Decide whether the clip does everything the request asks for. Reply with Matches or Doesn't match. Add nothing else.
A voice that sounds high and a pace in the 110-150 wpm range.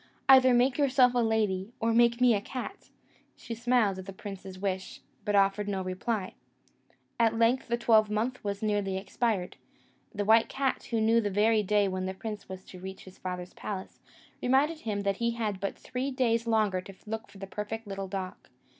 Doesn't match